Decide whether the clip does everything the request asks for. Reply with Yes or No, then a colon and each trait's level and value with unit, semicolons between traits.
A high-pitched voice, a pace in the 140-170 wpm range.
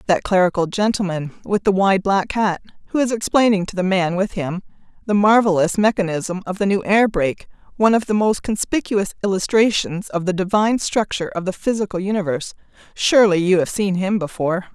No: high, 195 Hz; average, 180 wpm